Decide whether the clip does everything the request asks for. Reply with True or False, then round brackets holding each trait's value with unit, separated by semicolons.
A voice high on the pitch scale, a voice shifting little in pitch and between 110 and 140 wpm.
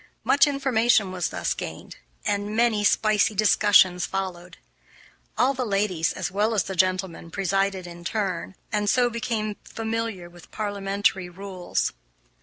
False (200 Hz; 3.0 semitones; 135 wpm)